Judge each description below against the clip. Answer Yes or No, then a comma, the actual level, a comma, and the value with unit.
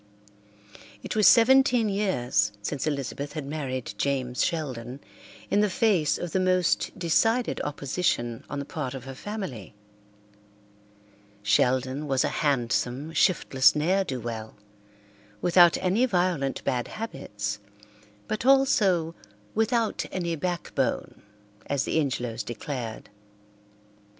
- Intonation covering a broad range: Yes, wide, 6.6 semitones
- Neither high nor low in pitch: Yes, medium, 150 Hz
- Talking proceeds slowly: Yes, slow, 115 wpm